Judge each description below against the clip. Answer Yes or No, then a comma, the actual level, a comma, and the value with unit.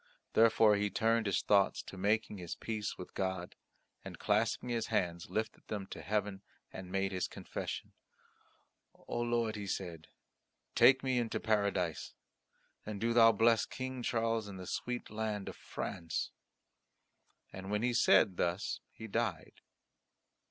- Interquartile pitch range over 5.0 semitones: No, average, 2.9 semitones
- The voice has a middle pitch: No, low, 105 Hz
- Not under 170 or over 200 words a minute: No, average, 150 wpm